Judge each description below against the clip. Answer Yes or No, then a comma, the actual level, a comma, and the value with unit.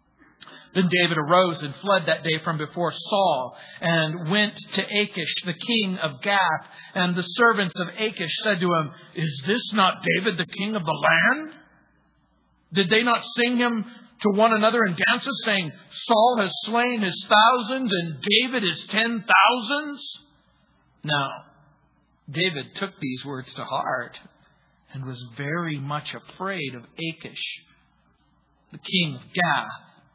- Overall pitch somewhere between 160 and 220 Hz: Yes, high, 190 Hz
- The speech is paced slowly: No, average, 145 wpm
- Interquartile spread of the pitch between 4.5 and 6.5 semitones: Yes, average, 5.0 semitones